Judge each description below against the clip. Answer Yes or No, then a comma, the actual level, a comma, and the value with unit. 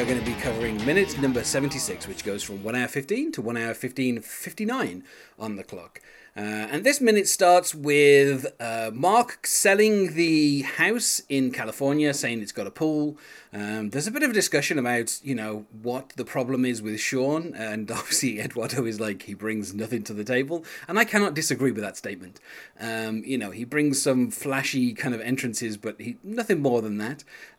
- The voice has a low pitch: Yes, low, 130 Hz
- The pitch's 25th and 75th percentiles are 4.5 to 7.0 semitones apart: Yes, average, 5.1 semitones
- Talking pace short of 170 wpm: No, average, 195 wpm